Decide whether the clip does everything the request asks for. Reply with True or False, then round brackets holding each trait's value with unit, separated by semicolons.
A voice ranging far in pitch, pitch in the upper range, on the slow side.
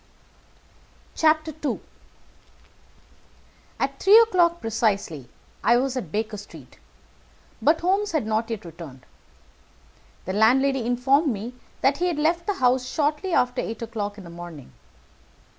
True (6.6 semitones; 250 Hz; 125 wpm)